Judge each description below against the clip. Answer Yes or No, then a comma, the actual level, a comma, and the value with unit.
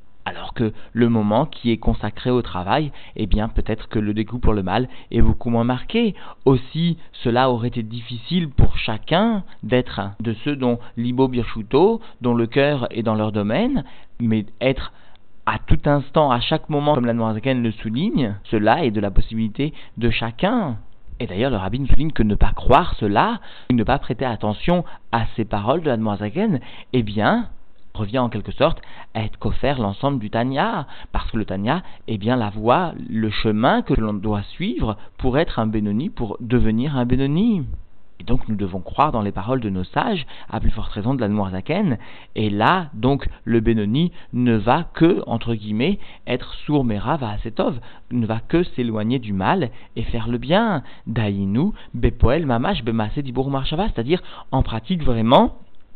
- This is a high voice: No, low, 115 Hz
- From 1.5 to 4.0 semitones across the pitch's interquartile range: Yes, average, 3.6 semitones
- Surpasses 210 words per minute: No, average, 180 wpm